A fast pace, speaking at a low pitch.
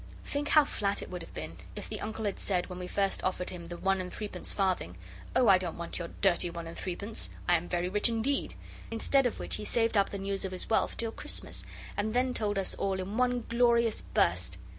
No: fast, 235 wpm; high, 200 Hz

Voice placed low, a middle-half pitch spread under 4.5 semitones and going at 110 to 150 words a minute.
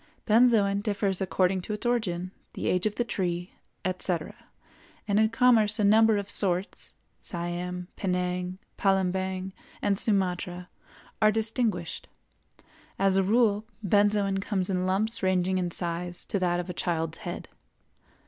No: high, 190 Hz; average, 2.7 semitones; average, 140 wpm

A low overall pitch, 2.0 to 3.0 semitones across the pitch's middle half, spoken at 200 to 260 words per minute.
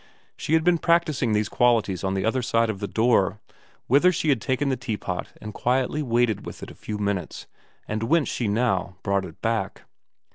No: low, 115 Hz; average, 4.4 semitones; fast, 205 wpm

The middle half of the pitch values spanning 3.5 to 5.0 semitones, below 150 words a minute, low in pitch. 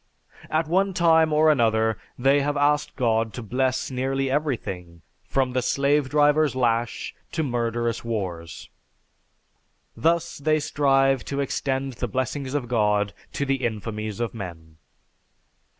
Yes: average, 4.3 semitones; slow, 135 wpm; low, 130 Hz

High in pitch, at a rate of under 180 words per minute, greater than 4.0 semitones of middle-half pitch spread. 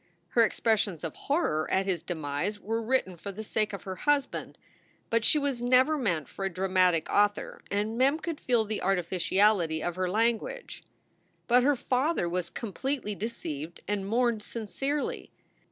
Yes: high, 210 Hz; average, 165 wpm; average, 5.1 semitones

